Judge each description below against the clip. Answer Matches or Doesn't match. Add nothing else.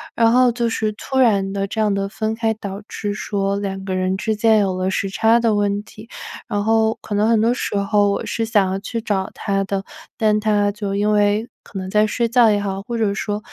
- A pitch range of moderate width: Doesn't match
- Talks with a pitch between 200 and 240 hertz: Matches